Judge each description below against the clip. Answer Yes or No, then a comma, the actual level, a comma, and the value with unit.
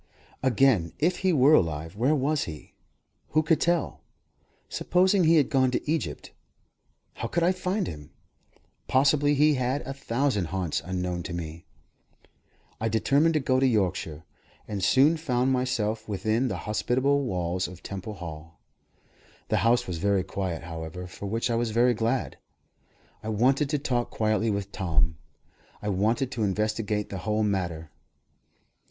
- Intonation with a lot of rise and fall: Yes, wide, 6.7 semitones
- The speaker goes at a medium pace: Yes, average, 155 wpm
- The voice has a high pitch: No, low, 110 Hz